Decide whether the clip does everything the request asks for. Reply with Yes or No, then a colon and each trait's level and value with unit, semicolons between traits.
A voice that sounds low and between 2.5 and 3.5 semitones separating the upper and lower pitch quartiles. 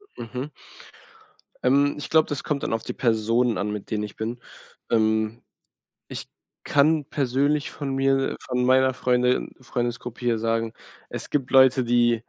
Yes: low, 125 Hz; average, 2.9 semitones